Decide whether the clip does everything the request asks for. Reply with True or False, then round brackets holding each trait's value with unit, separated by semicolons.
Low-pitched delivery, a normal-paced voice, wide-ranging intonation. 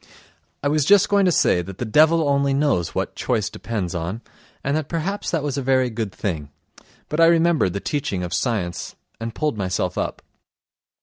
True (130 Hz; 190 wpm; 8.0 semitones)